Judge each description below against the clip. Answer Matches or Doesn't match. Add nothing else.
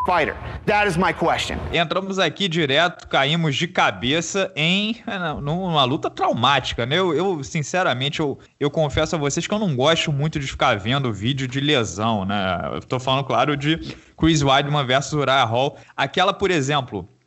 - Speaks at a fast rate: Doesn't match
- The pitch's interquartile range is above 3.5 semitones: Matches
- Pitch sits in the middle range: Matches